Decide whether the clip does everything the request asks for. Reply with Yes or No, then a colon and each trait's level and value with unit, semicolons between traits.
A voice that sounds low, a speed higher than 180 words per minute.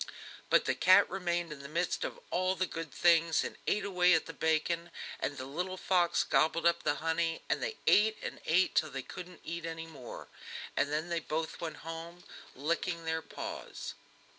No: medium, 165 Hz; average, 190 wpm